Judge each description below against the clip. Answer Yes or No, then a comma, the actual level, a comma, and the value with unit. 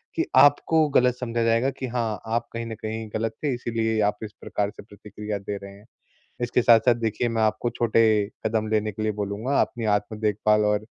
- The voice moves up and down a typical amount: No, narrow, 1.9 semitones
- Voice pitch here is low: Yes, low, 110 Hz